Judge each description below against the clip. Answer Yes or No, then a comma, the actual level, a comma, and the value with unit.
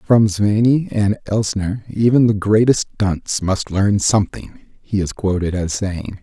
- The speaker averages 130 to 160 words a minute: Yes, average, 155 wpm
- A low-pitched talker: Yes, low, 105 Hz